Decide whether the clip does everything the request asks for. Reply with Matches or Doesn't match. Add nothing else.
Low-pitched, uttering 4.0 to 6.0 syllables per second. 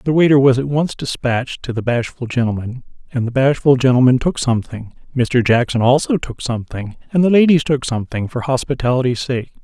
Matches